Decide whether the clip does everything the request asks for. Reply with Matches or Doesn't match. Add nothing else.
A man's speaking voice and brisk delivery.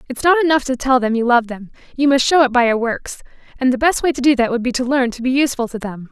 Doesn't match